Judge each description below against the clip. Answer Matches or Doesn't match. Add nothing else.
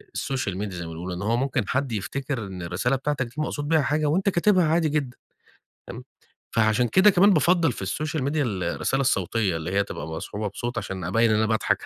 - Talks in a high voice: Doesn't match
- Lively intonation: Matches